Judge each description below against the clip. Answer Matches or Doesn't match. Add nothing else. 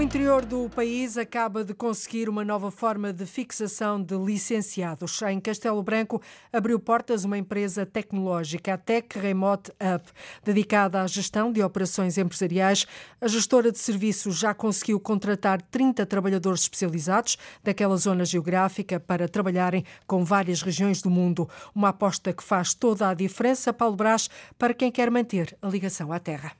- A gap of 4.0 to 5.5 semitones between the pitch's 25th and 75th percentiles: Doesn't match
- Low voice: Doesn't match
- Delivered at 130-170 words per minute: Matches